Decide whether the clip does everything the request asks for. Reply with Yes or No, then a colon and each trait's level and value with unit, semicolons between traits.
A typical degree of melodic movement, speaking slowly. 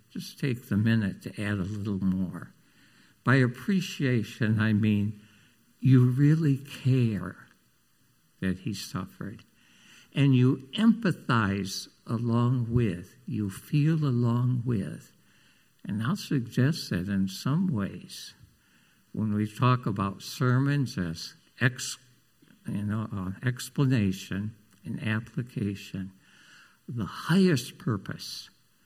Yes: average, 4.8 semitones; slow, 105 wpm